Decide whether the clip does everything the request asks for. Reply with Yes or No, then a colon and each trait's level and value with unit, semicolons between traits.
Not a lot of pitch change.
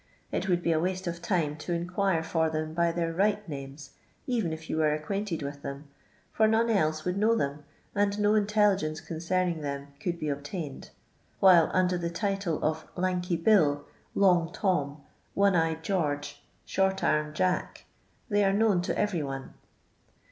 No: average, 3.9 semitones